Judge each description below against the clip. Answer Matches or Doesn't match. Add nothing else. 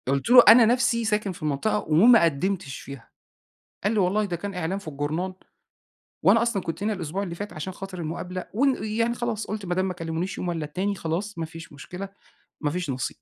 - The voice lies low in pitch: Doesn't match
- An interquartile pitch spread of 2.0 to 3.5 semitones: Doesn't match